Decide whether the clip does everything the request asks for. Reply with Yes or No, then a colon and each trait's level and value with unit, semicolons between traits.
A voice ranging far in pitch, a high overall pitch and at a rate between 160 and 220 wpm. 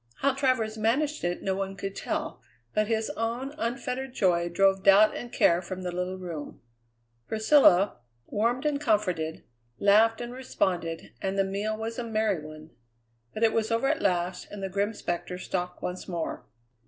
No: average, 4.0 semitones; high, 205 Hz; average, 170 wpm